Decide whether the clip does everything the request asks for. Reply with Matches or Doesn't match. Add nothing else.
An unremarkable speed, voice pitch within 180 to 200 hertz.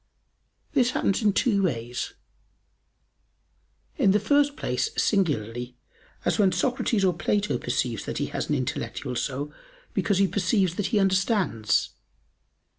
Doesn't match